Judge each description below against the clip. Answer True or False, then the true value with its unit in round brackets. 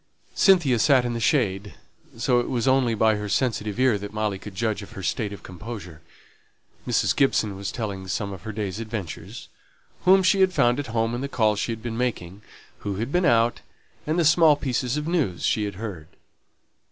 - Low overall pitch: True (115 Hz)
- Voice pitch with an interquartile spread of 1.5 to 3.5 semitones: False (4.3 semitones)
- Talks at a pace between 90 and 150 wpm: False (200 wpm)